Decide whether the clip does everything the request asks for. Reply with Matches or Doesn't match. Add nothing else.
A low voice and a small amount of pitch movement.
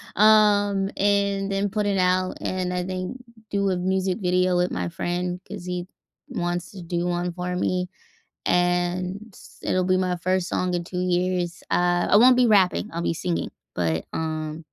Doesn't match